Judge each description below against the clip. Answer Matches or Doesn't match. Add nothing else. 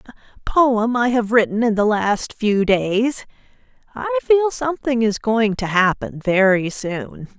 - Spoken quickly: Doesn't match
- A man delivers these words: Doesn't match